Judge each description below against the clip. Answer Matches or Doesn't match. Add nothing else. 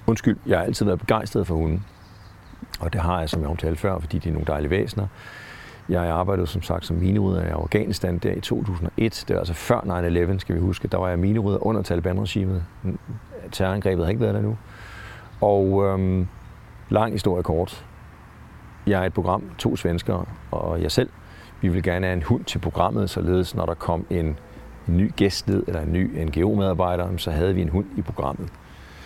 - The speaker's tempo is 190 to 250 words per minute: Matches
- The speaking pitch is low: Matches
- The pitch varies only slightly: Doesn't match